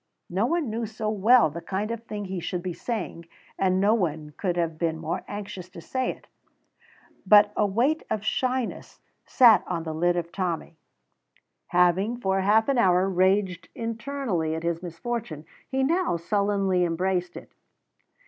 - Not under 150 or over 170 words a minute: Yes, average, 165 wpm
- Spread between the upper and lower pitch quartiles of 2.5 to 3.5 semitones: No, average, 4.3 semitones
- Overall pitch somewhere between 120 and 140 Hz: No, high, 190 Hz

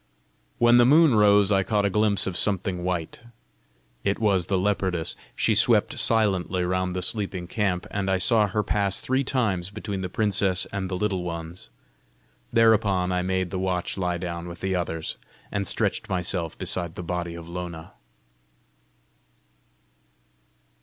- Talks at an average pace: Yes, average, 155 wpm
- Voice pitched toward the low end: Yes, very low, 95 Hz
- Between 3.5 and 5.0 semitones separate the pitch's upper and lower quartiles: No, narrow, 2.6 semitones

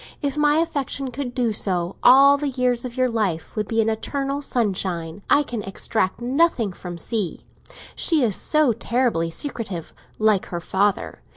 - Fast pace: No, average, 165 wpm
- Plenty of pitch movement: Yes, wide, 5.9 semitones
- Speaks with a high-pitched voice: Yes, high, 235 Hz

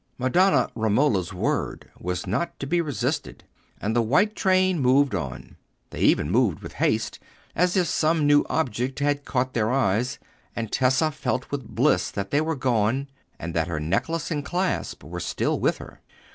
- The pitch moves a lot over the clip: Yes, wide, 6.3 semitones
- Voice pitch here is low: Yes, low, 130 Hz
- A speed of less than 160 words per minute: No, average, 170 wpm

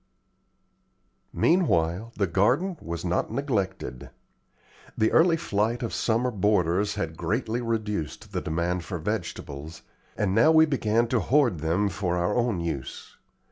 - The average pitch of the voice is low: Yes, low, 105 Hz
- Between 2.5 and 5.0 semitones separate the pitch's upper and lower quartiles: No, wide, 5.6 semitones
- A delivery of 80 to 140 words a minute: Yes, slow, 135 wpm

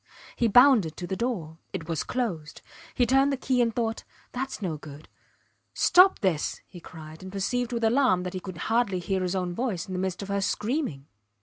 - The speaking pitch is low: No, high, 195 Hz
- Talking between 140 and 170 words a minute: No, fast, 205 wpm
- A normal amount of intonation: No, wide, 5.7 semitones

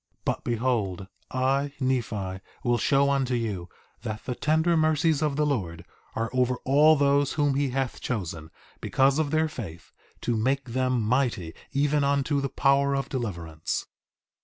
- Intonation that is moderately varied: Yes, average, 3.9 semitones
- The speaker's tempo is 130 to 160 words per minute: Yes, average, 155 wpm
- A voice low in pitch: Yes, low, 130 Hz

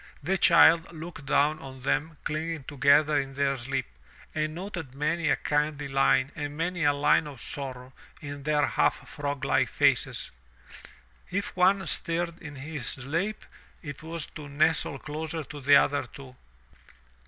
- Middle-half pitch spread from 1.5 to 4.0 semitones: Yes, narrow, 2.6 semitones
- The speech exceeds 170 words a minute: No, average, 155 wpm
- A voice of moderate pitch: Yes, medium, 150 Hz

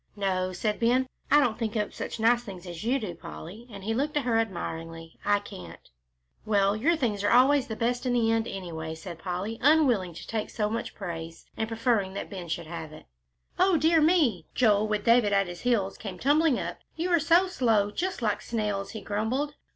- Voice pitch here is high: Yes, high, 215 Hz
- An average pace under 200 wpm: No, fast, 205 wpm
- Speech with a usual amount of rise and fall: Yes, average, 4.6 semitones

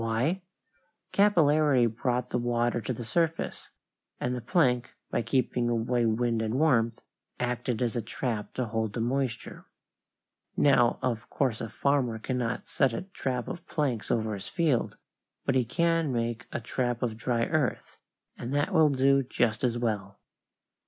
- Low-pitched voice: Yes, low, 125 Hz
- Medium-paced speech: Yes, average, 160 wpm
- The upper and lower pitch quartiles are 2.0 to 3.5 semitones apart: Yes, average, 3.0 semitones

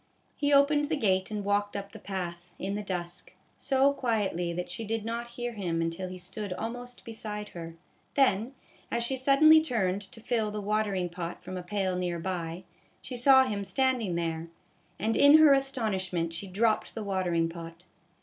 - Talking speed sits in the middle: Yes, average, 185 wpm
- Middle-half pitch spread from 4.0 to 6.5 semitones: Yes, average, 4.9 semitones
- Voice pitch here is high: Yes, high, 205 Hz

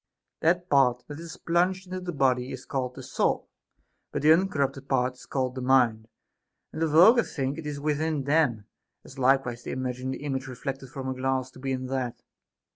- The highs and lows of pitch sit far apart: No, average, 3.3 semitones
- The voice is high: No, low, 135 Hz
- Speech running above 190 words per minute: Yes, average, 200 wpm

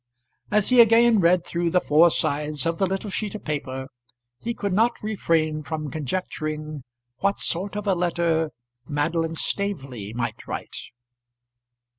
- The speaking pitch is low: No, medium, 170 Hz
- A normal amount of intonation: Yes, average, 4.7 semitones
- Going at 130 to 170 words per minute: Yes, average, 145 wpm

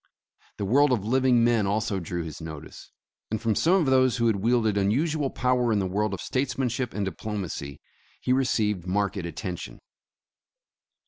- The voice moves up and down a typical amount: Yes, average, 4.7 semitones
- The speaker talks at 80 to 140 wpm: No, average, 165 wpm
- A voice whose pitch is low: Yes, low, 110 Hz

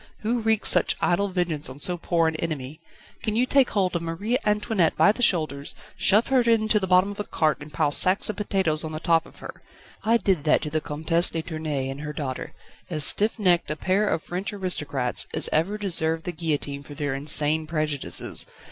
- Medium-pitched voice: Yes, medium, 165 Hz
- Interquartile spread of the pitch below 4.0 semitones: No, average, 4.9 semitones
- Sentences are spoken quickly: Yes, fast, 210 wpm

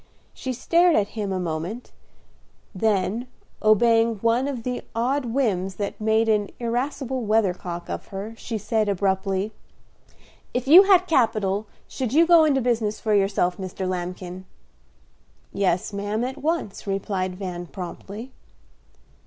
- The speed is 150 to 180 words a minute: No, slow, 135 wpm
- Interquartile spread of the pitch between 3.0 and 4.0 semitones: No, average, 4.4 semitones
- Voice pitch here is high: Yes, high, 215 Hz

